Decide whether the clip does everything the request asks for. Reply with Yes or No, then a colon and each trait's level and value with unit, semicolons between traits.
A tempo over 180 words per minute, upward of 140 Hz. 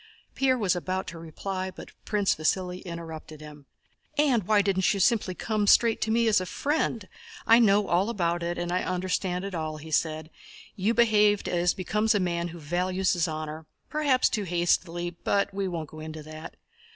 Yes: average, 190 wpm; medium, 185 Hz